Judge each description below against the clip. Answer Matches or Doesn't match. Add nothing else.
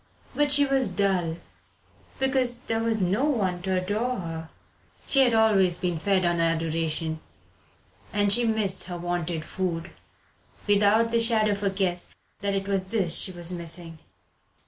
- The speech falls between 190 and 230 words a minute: Doesn't match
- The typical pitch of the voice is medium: Doesn't match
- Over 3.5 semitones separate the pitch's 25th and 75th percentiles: Matches